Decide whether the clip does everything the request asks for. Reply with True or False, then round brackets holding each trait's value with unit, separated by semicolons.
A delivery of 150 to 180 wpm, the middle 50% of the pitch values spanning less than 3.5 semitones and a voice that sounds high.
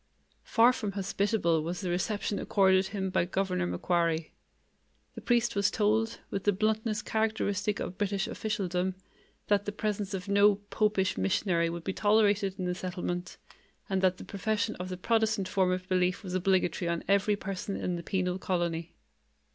True (165 wpm; 2.4 semitones; 195 Hz)